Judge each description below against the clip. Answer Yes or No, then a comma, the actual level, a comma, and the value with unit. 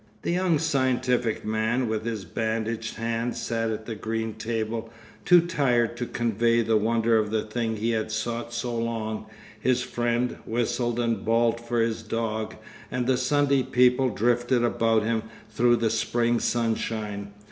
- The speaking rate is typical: Yes, average, 160 wpm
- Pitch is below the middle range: Yes, low, 115 Hz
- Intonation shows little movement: Yes, narrow, 1.5 semitones